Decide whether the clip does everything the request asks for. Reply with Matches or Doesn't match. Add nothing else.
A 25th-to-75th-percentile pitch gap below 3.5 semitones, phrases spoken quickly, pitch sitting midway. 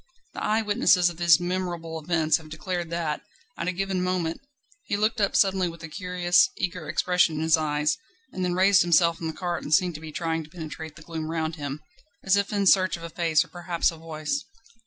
Matches